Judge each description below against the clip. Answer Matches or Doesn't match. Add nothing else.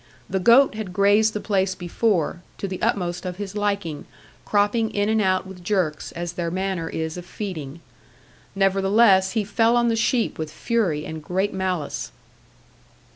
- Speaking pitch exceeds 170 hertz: Matches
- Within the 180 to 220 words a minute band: Doesn't match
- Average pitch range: Matches